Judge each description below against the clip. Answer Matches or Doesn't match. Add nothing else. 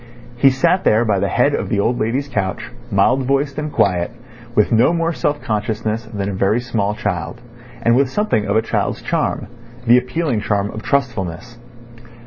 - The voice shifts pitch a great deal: Doesn't match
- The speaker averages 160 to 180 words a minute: Matches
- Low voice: Matches